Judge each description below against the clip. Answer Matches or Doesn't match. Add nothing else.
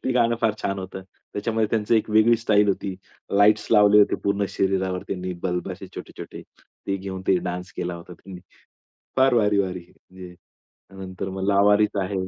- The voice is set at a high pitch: Doesn't match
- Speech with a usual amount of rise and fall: Doesn't match